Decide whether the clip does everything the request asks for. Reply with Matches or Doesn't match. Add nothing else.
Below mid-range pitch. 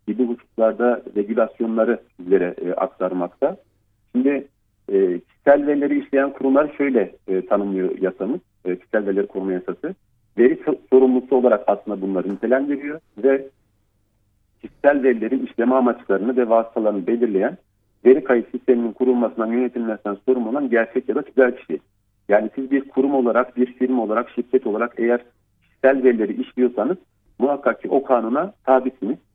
Matches